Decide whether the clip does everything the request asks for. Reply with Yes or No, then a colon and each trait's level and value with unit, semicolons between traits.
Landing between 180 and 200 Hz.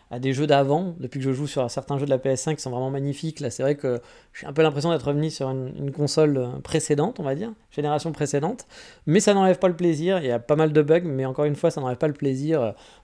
No: medium, 145 Hz